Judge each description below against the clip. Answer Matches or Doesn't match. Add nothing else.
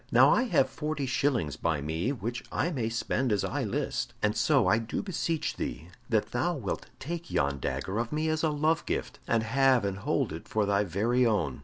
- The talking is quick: Matches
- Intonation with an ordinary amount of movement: Doesn't match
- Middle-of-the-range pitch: Doesn't match